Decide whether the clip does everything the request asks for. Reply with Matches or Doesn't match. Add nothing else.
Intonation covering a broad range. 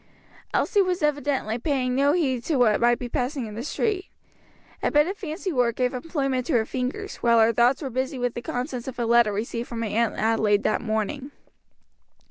Doesn't match